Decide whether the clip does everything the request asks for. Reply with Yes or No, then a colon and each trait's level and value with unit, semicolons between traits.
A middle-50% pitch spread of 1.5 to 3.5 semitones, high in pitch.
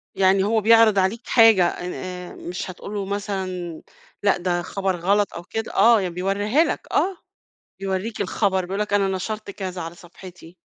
Yes: narrow, 2.4 semitones; high, 195 Hz